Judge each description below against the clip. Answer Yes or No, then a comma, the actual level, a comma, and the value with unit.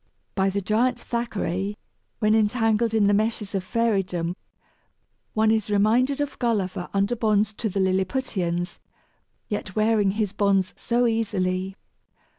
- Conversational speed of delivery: No, slow, 130 wpm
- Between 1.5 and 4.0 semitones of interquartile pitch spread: Yes, average, 2.7 semitones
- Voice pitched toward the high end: Yes, high, 210 Hz